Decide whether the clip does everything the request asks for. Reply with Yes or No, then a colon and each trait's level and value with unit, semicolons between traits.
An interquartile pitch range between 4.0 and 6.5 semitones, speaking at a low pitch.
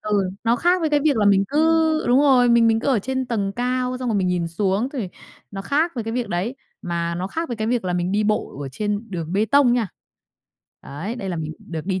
No: average, 5.2 semitones; high, 220 Hz